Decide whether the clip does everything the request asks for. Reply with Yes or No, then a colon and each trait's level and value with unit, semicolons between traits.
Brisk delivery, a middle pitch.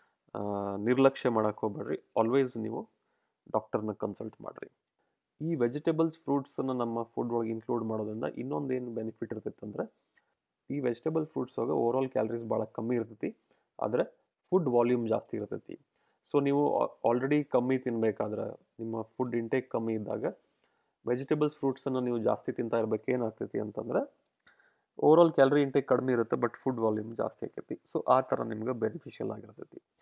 No: fast, 140 wpm; low, 120 Hz